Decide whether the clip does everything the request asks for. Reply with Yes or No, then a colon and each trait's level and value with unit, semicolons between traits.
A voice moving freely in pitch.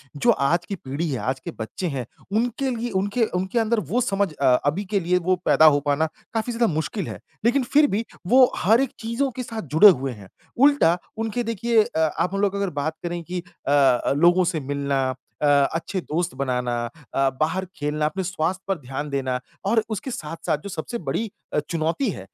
Yes: wide, 7.2 semitones